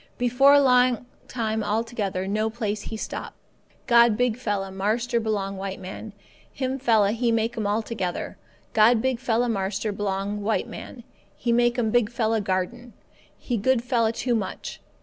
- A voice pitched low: No, high, 225 Hz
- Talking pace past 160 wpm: No, average, 155 wpm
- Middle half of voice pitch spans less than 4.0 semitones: Yes, average, 2.8 semitones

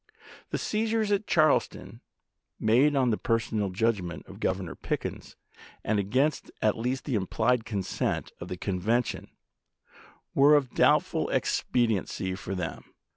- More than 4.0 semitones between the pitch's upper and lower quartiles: Yes, wide, 5.4 semitones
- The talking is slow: Yes, slow, 130 wpm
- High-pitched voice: No, low, 115 Hz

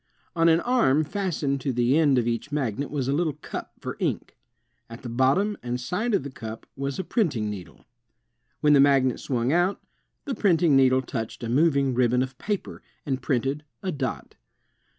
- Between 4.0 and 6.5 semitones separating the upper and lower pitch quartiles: Yes, average, 4.6 semitones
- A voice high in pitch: No, medium, 140 Hz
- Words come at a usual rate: Yes, average, 185 wpm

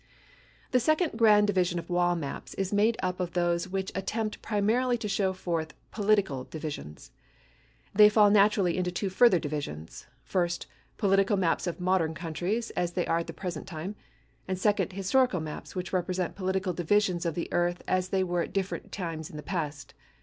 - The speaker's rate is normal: Yes, average, 180 wpm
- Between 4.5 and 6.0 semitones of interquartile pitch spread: No, average, 2.9 semitones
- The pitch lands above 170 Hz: Yes, medium, 185 Hz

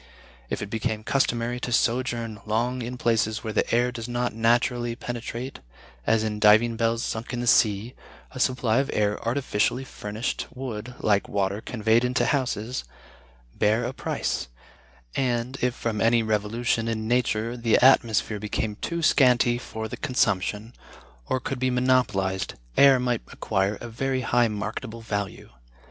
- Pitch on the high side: No, low, 115 Hz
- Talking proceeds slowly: No, average, 155 wpm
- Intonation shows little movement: Yes, narrow, 2.3 semitones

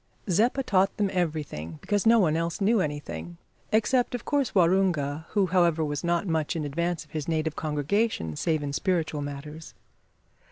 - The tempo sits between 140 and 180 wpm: Yes, average, 165 wpm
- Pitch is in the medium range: Yes, medium, 165 Hz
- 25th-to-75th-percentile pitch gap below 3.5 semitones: No, average, 4.6 semitones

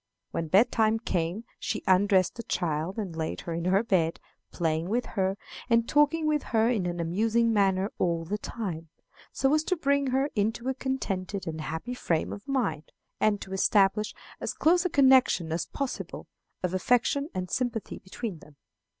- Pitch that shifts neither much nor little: No, wide, 5.9 semitones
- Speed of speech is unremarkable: Yes, average, 175 wpm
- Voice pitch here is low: No, high, 205 Hz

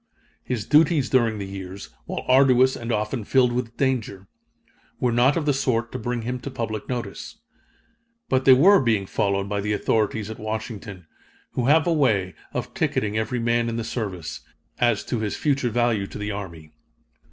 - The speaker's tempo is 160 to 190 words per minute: Yes, average, 180 wpm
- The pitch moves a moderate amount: Yes, average, 3.6 semitones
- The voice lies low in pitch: Yes, low, 115 Hz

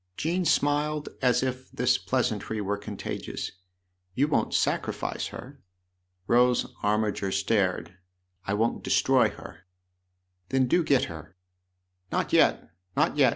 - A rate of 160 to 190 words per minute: No, average, 140 wpm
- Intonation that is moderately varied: No, wide, 6.1 semitones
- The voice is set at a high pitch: No, low, 105 Hz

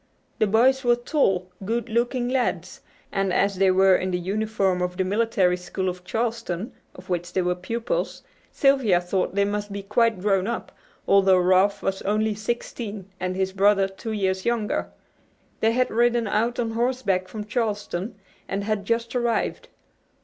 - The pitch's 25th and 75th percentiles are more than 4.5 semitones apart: No, average, 3.7 semitones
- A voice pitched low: No, high, 205 Hz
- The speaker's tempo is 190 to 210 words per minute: No, average, 165 wpm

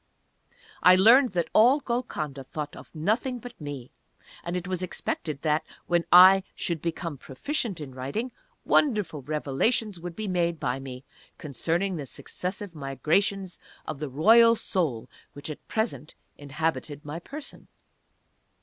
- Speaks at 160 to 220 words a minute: No, average, 140 wpm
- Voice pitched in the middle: Yes, medium, 170 Hz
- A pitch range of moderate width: No, wide, 5.9 semitones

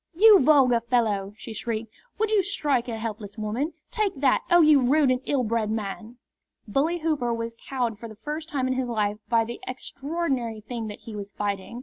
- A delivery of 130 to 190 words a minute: No, average, 200 wpm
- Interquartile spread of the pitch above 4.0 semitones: Yes, average, 4.9 semitones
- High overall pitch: Yes, high, 240 Hz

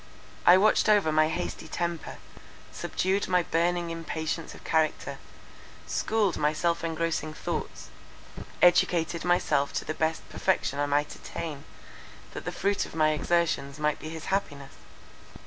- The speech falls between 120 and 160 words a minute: Yes, average, 140 wpm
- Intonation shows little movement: Yes, narrow, 2.2 semitones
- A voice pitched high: No, medium, 165 Hz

